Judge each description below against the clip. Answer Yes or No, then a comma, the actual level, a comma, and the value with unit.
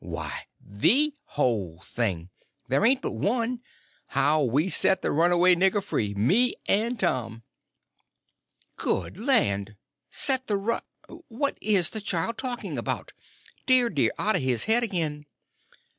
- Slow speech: Yes, slow, 130 wpm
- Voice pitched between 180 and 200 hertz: Yes, medium, 185 Hz